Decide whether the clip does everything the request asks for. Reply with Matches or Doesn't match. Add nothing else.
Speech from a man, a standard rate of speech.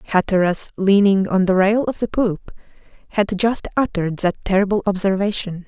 Doesn't match